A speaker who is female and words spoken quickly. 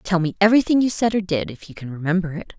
Yes: female; fast, 280 wpm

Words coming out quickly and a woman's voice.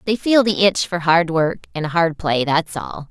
Yes: fast, 230 wpm; female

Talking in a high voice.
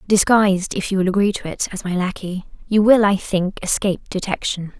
Yes: high, 195 Hz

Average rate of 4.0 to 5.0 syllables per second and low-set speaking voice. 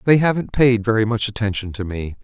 No: 5.9 syllables/s; low, 115 Hz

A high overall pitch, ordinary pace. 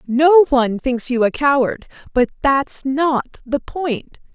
Yes: very high, 270 Hz; average, 150 wpm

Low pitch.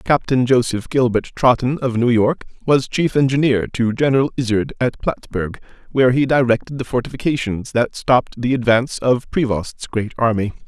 Yes: low, 125 Hz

